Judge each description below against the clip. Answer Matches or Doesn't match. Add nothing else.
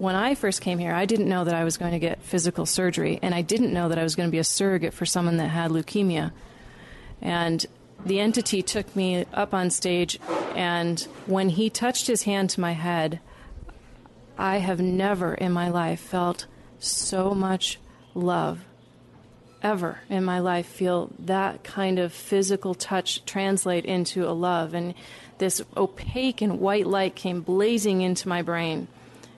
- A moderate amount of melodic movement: Doesn't match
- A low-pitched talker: Doesn't match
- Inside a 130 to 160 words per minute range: Doesn't match